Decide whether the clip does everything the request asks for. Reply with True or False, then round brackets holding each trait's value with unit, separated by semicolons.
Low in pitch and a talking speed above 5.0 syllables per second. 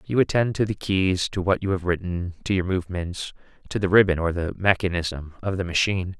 True (90 Hz; 5.6 syllables/s)